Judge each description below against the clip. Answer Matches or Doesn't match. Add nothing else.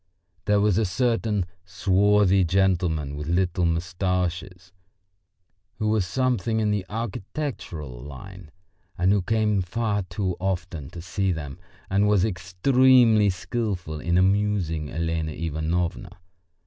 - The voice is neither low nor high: Doesn't match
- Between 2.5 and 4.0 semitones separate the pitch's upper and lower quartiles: Matches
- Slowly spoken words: Matches